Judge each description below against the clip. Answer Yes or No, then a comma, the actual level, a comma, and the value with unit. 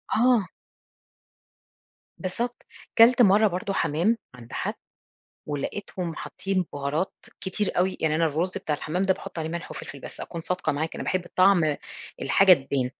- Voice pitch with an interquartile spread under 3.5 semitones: No, average, 3.8 semitones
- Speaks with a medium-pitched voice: Yes, medium, 180 Hz